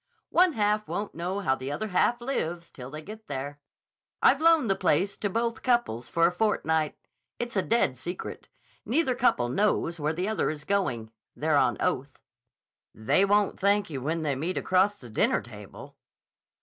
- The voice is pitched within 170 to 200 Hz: Yes, medium, 185 Hz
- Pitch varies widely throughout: Yes, wide, 6.5 semitones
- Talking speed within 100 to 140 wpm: No, average, 175 wpm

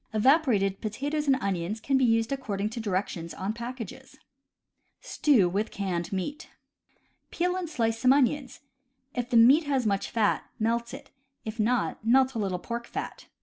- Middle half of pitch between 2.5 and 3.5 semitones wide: No, average, 4.4 semitones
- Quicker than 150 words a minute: Yes, average, 170 wpm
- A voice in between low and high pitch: No, high, 235 Hz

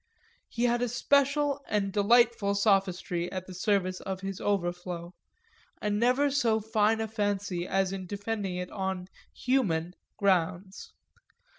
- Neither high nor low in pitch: No, high, 200 Hz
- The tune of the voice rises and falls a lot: No, average, 3.4 semitones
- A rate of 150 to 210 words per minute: No, slow, 135 wpm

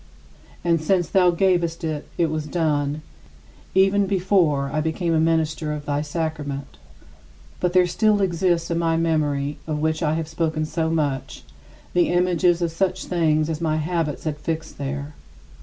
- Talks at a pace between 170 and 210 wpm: No, average, 160 wpm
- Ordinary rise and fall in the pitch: No, narrow, 2.3 semitones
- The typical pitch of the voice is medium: Yes, medium, 160 Hz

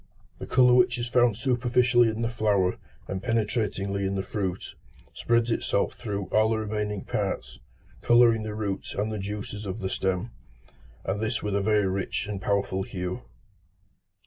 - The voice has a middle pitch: No, low, 105 Hz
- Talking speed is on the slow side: No, average, 165 wpm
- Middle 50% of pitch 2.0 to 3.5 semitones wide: Yes, average, 3.0 semitones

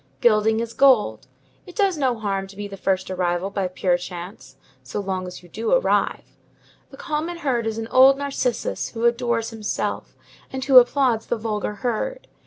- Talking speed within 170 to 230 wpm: Yes, average, 180 wpm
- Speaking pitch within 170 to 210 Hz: No, high, 225 Hz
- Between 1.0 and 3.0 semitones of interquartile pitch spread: No, average, 5.1 semitones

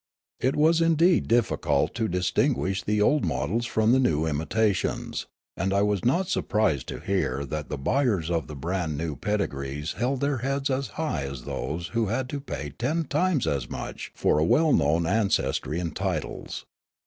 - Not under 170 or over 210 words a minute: Yes, average, 180 wpm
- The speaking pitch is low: Yes, low, 100 Hz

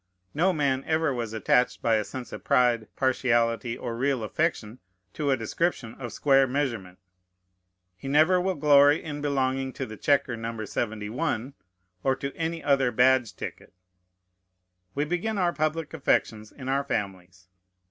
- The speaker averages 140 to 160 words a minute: Yes, average, 150 wpm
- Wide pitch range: No, average, 4.2 semitones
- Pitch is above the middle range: No, low, 130 Hz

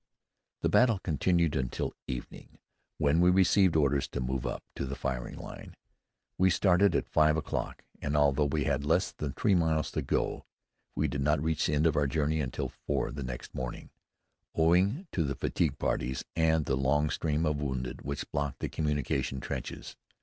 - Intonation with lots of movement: No, average, 2.9 semitones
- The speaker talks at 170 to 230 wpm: Yes, average, 180 wpm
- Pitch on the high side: No, very low, 75 Hz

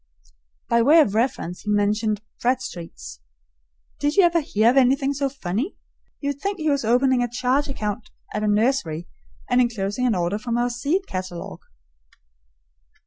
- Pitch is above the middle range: Yes, high, 240 Hz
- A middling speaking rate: Yes, average, 160 wpm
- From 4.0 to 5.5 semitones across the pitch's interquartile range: Yes, average, 4.8 semitones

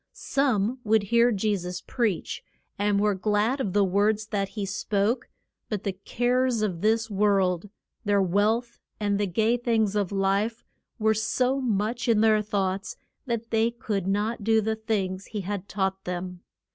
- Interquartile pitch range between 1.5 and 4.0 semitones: Yes, narrow, 2.4 semitones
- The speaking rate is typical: Yes, average, 165 wpm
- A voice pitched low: No, high, 210 Hz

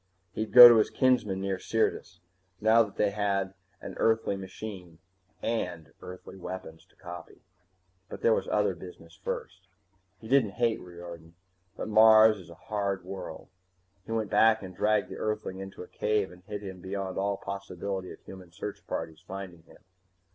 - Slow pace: No, average, 170 wpm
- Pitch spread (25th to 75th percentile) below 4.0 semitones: Yes, average, 2.9 semitones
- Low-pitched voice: Yes, low, 100 Hz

